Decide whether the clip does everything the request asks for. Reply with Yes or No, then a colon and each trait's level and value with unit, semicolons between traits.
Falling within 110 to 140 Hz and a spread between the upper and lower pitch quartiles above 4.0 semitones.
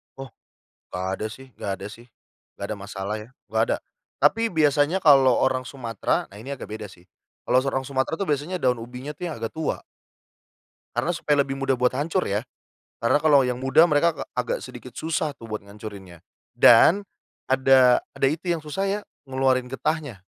Yes: low, 135 Hz; average, 4.8 semitones